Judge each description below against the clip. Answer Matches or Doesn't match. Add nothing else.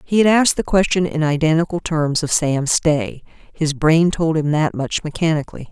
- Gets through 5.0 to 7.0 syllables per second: Matches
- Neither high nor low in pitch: Matches